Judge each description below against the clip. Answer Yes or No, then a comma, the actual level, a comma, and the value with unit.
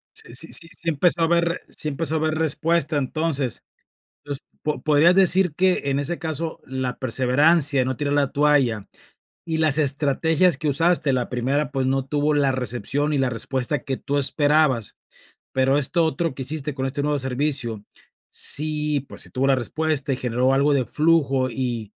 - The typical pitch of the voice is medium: Yes, medium, 145 Hz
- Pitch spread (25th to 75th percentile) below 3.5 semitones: Yes, average, 3.1 semitones